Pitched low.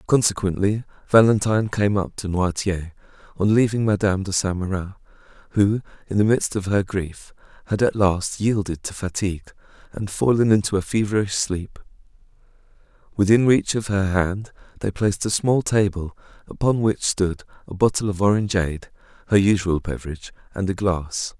Yes: low, 100 Hz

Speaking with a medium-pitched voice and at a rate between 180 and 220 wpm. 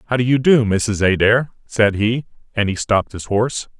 No: low, 110 Hz; fast, 205 wpm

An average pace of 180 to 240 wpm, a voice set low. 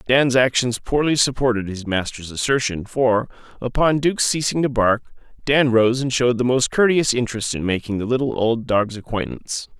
No: average, 170 wpm; low, 120 Hz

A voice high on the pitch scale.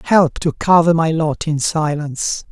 No: medium, 160 Hz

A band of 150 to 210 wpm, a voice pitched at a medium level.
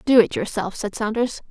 No: average, 200 wpm; high, 225 Hz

